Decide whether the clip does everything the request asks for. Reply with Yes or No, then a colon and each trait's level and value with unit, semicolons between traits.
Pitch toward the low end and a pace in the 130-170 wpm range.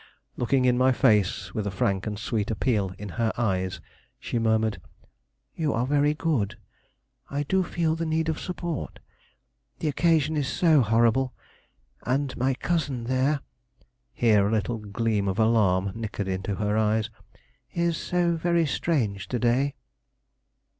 Yes: low, 120 Hz; average, 145 wpm